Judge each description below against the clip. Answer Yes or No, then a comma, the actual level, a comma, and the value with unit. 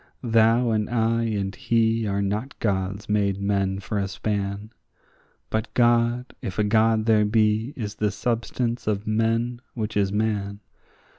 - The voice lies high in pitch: No, low, 110 Hz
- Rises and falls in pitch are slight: Yes, narrow, 2.2 semitones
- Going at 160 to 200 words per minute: No, average, 150 wpm